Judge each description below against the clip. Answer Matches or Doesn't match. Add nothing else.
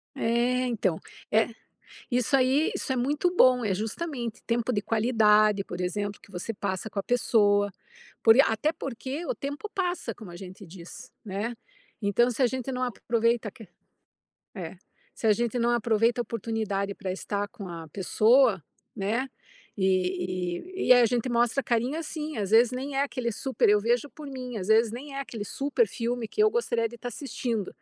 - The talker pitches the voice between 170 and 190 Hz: Doesn't match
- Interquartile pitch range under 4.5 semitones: Matches